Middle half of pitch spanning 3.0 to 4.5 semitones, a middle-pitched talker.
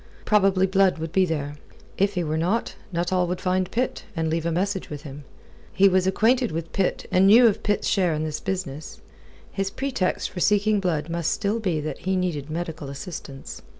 Yes: average, 3.5 semitones; medium, 180 Hz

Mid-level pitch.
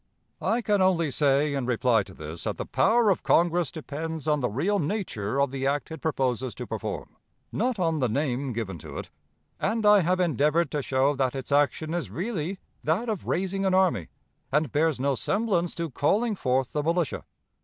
Yes: medium, 155 Hz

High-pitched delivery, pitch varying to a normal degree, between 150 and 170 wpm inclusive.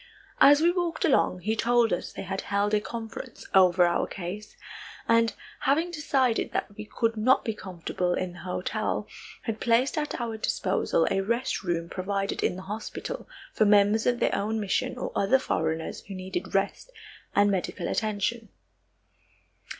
Yes: high, 215 Hz; average, 3.9 semitones; average, 165 wpm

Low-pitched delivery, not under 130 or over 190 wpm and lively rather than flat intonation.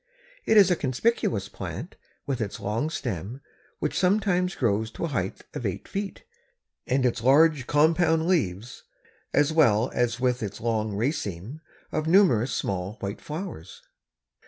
Yes: low, 130 Hz; average, 145 wpm; wide, 7.2 semitones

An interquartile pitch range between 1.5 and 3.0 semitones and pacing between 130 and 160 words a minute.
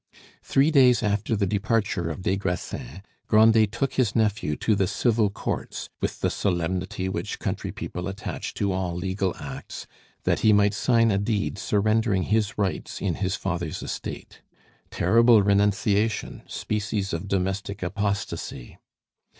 Yes: narrow, 2.5 semitones; average, 140 wpm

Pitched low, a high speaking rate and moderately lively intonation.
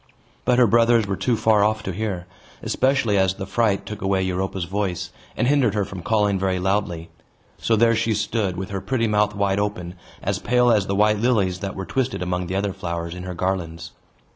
Yes: low, 100 Hz; fast, 210 wpm; average, 3.0 semitones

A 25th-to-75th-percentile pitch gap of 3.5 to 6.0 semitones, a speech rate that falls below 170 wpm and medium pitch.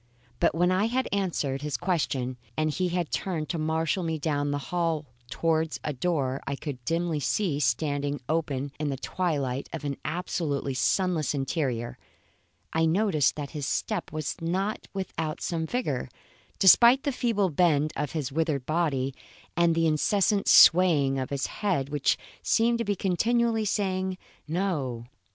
Yes: average, 4.4 semitones; average, 155 wpm; medium, 160 Hz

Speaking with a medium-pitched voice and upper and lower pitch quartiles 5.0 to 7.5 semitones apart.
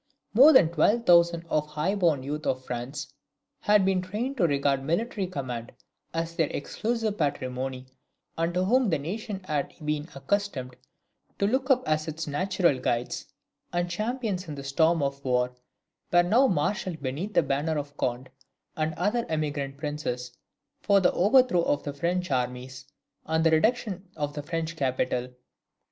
Yes: medium, 160 Hz; wide, 5.6 semitones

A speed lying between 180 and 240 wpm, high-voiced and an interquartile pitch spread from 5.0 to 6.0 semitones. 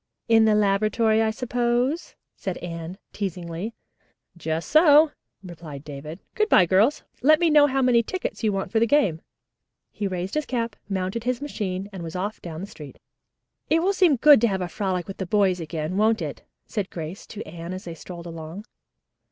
Yes: average, 190 wpm; high, 200 Hz; wide, 5.5 semitones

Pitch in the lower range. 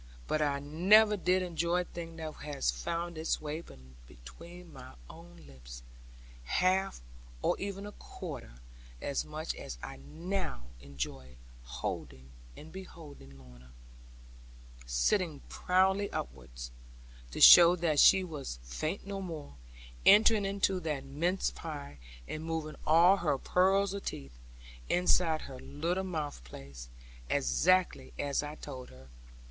No: medium, 155 Hz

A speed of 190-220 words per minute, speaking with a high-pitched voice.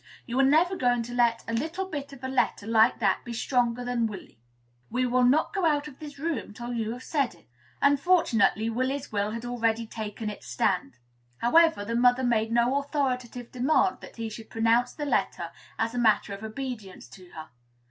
Yes: average, 200 wpm; high, 245 Hz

